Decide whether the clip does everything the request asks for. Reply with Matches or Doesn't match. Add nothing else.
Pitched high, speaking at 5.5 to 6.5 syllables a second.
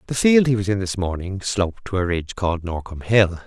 Doesn't match